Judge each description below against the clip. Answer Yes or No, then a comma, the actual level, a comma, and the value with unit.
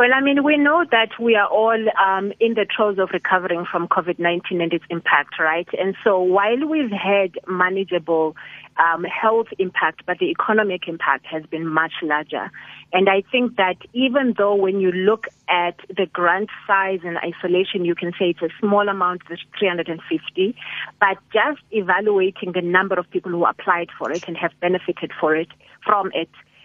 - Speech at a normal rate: Yes, average, 185 wpm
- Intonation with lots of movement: No, average, 3.1 semitones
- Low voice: No, medium, 185 Hz